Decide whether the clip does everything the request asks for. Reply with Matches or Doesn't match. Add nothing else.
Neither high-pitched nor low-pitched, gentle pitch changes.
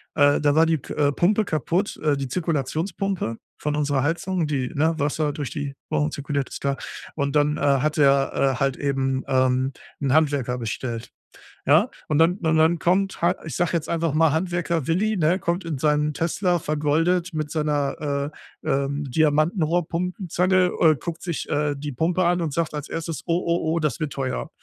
Doesn't match